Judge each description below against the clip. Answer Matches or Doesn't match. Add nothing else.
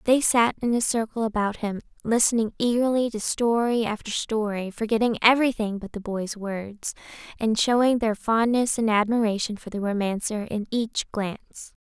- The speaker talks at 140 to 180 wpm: Matches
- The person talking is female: Matches